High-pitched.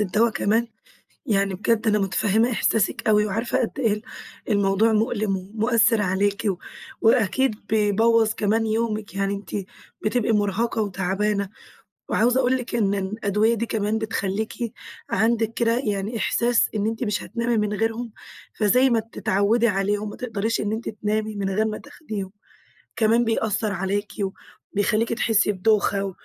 Yes: high, 215 Hz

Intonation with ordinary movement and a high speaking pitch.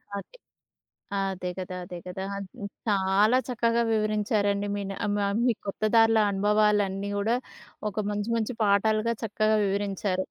No: narrow, 1.6 semitones; high, 205 Hz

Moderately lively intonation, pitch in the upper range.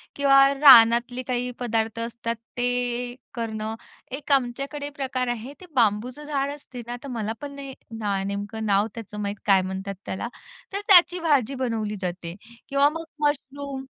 Yes: average, 4.2 semitones; high, 245 Hz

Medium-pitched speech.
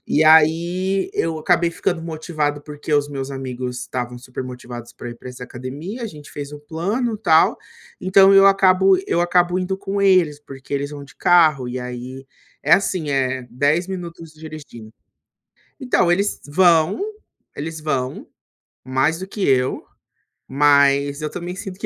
Yes: medium, 155 Hz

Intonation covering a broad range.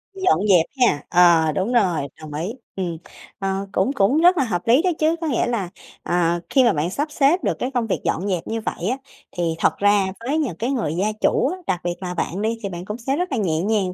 Yes: wide, 6.4 semitones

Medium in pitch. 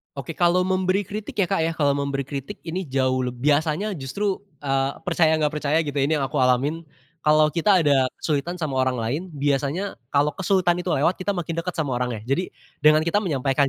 Yes: medium, 150 Hz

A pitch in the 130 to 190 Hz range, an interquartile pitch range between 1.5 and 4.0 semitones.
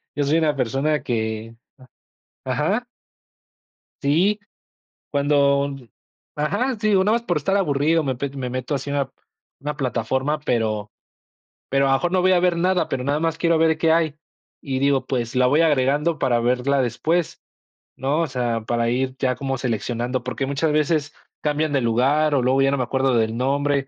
Yes: medium, 140 Hz; average, 3.5 semitones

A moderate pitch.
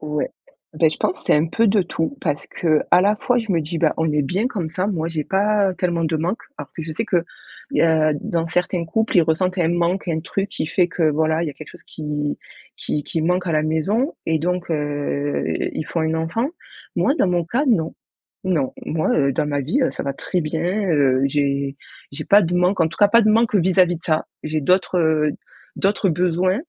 Yes: medium, 165 Hz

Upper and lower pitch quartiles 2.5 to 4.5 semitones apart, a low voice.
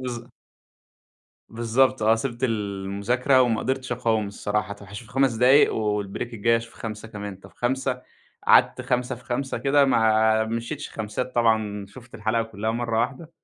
Yes: average, 2.8 semitones; low, 115 Hz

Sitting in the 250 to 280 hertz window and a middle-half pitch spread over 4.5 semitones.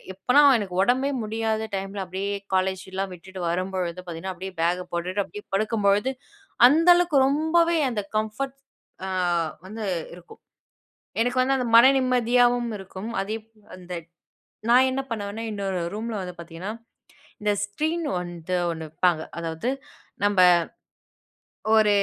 No: high, 205 Hz; average, 4.9 semitones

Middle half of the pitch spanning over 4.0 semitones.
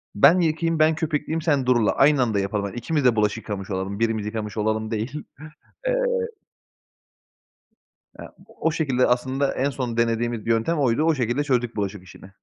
Yes: average, 5.2 semitones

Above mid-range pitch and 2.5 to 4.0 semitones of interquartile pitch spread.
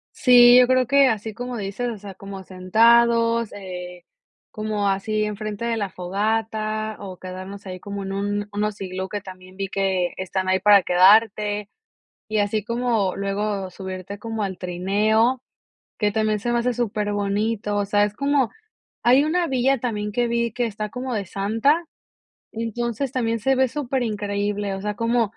Yes: high, 210 Hz; average, 2.9 semitones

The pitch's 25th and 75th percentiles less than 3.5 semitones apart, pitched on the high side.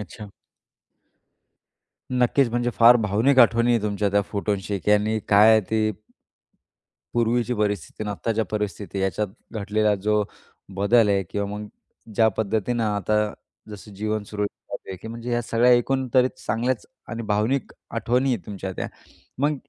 No: narrow, 2.5 semitones; low, 110 Hz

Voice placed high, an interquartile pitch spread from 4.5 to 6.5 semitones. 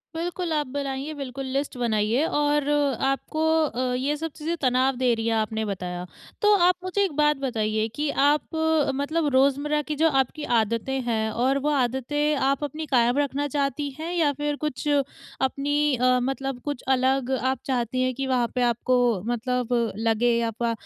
No: very high, 270 Hz; average, 3.2 semitones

